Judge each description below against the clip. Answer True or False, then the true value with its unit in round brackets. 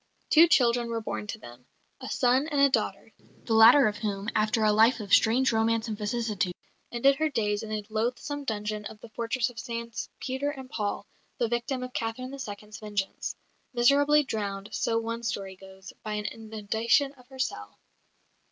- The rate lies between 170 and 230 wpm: True (180 wpm)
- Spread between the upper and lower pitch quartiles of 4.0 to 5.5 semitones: False (3.3 semitones)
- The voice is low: False (225 Hz)